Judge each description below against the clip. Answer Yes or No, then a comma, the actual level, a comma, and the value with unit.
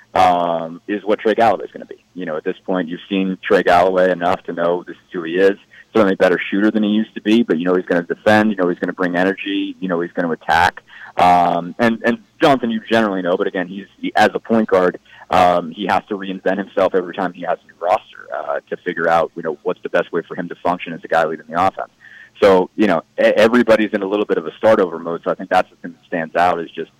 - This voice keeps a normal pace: No, fast, 280 wpm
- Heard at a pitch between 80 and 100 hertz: Yes, very low, 95 Hz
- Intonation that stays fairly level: No, average, 3.4 semitones